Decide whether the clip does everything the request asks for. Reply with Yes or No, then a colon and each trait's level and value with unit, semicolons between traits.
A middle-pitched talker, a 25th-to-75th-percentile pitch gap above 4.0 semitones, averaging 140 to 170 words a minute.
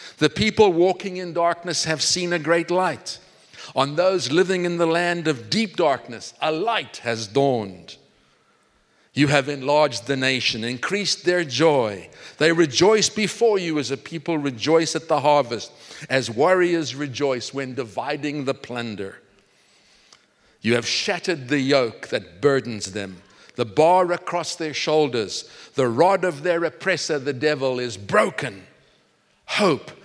Yes: medium, 150 Hz; average, 4.8 semitones; average, 145 wpm